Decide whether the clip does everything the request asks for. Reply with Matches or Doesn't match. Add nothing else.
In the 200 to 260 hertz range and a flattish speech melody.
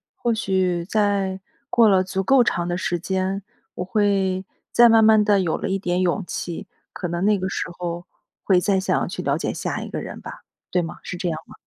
Doesn't match